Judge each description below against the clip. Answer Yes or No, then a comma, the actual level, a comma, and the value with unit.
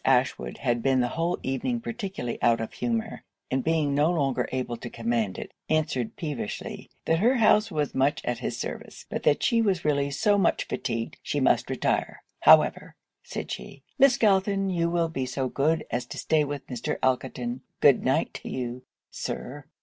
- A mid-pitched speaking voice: Yes, medium, 145 Hz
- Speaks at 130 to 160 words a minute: No, average, 180 wpm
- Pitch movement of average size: No, wide, 5.9 semitones